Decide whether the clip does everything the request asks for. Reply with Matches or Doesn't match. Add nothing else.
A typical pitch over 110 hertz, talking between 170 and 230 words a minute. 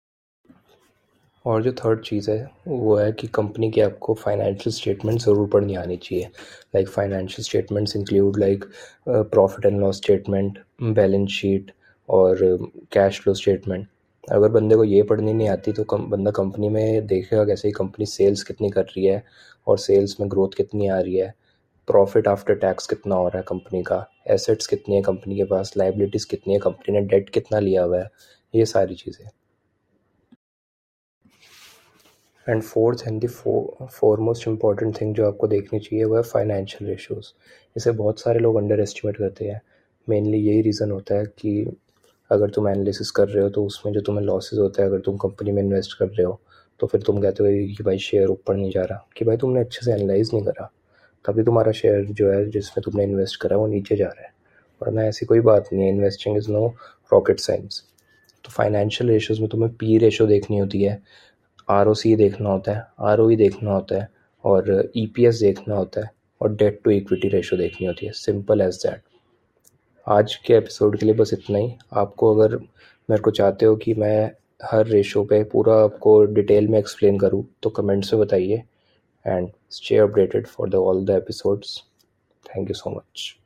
Doesn't match